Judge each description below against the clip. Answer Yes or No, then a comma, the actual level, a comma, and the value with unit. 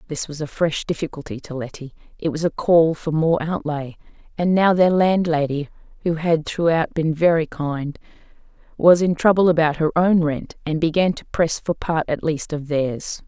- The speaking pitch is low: No, medium, 160 Hz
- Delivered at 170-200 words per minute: Yes, average, 185 wpm